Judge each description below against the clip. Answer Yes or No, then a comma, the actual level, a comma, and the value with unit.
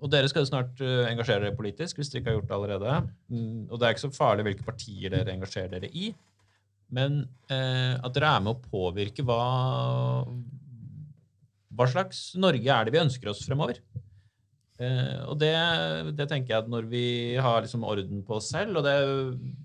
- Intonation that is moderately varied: Yes, average, 4.7 semitones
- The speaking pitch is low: Yes, low, 125 Hz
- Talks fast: No, average, 185 wpm